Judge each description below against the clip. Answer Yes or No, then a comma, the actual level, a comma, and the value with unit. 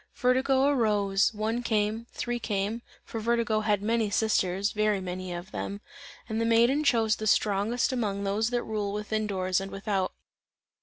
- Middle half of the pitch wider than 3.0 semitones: No, narrow, 2.6 semitones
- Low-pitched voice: No, high, 215 Hz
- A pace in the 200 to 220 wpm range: No, average, 160 wpm